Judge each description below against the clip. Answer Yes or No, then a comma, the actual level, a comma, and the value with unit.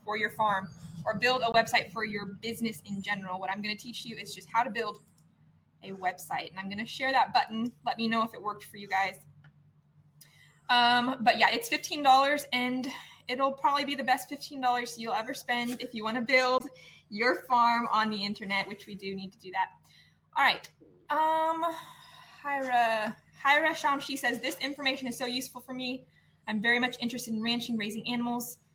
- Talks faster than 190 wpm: Yes, average, 200 wpm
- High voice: Yes, high, 235 Hz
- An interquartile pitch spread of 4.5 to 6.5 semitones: No, average, 3.9 semitones